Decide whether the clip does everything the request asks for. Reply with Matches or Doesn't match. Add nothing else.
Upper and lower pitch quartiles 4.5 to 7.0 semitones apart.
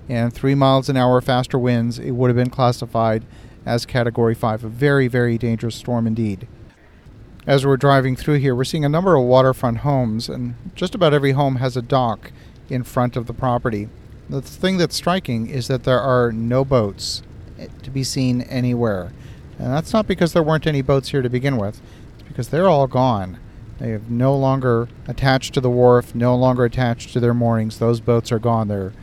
Doesn't match